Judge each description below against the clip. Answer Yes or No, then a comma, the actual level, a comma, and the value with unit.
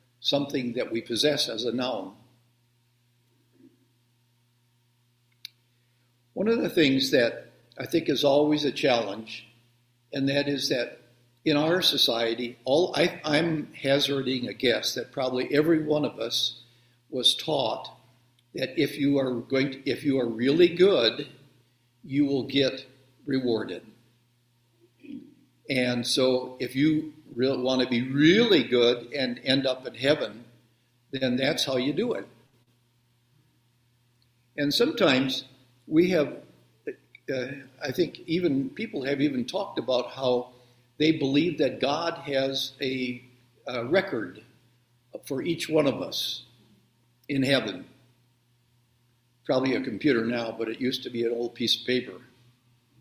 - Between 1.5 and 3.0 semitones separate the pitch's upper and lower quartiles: Yes, narrow, 2.5 semitones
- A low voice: Yes, low, 125 Hz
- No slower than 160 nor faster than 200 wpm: No, slow, 135 wpm